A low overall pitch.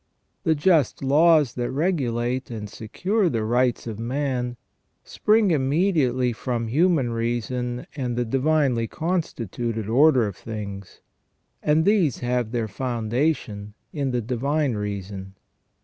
Yes: low, 125 Hz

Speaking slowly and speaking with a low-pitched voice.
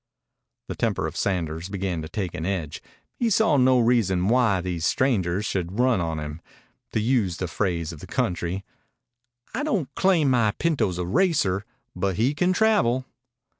No: average, 170 wpm; low, 100 Hz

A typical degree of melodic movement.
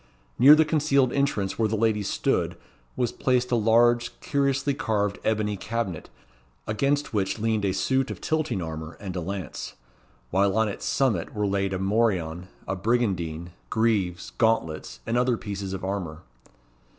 Yes: average, 4.0 semitones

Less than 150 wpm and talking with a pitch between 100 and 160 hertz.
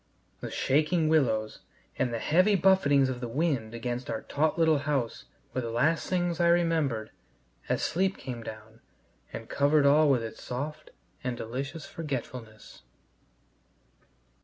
Yes: average, 140 wpm; medium, 140 Hz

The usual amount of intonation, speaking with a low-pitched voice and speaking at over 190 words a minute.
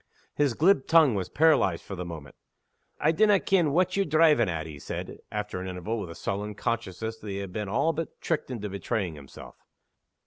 No: wide, 8.9 semitones; low, 110 Hz; average, 200 wpm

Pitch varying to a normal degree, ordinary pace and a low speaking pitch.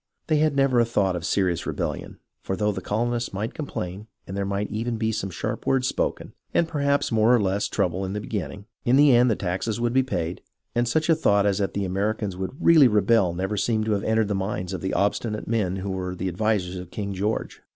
No: average, 3.7 semitones; fast, 235 wpm; low, 105 Hz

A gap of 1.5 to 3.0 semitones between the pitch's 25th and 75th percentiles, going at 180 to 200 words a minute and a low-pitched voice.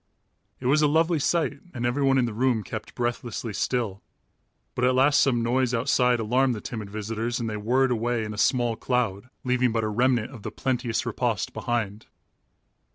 Yes: narrow, 2.5 semitones; average, 185 wpm; low, 120 Hz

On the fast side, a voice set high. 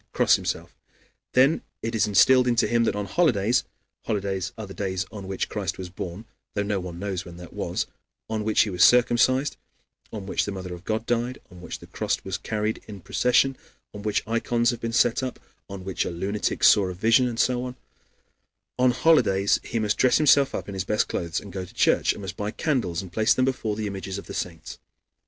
No: fast, 220 wpm; low, 105 Hz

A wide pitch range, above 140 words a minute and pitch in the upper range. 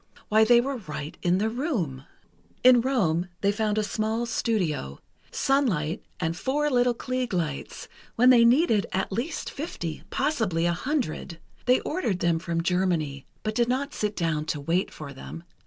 Yes: wide, 6.9 semitones; average, 160 wpm; high, 210 Hz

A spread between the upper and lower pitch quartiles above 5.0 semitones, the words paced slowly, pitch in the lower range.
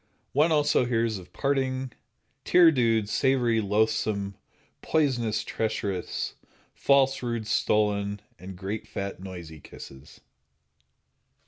No: average, 4.6 semitones; slow, 100 wpm; low, 110 Hz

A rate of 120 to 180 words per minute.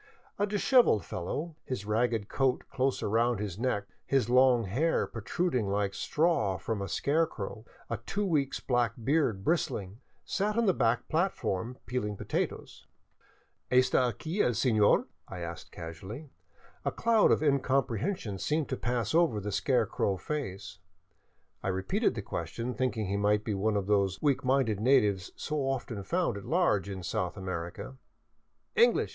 Yes: average, 160 wpm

